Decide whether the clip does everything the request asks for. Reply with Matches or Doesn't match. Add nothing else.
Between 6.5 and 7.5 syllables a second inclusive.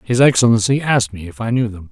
Matches